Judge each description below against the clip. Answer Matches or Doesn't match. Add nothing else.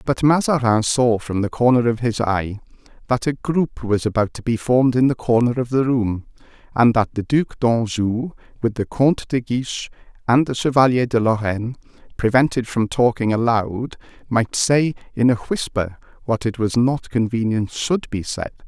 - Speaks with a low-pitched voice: Matches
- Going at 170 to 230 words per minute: Matches